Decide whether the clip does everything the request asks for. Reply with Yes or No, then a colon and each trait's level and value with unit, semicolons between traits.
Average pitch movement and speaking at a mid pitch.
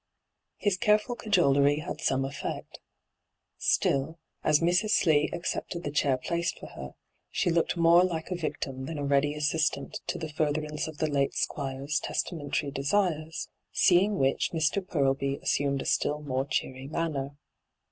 Yes: average, 3.4 semitones; medium, 150 Hz